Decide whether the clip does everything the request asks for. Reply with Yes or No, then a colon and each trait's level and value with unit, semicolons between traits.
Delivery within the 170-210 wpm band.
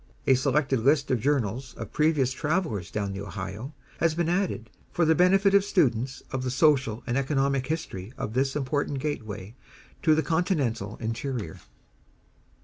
No: average, 155 wpm